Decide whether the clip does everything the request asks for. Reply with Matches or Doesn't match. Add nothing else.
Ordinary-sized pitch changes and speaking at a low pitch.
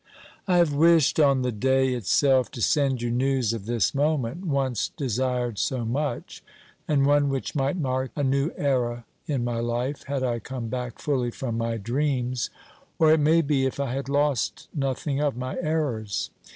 Matches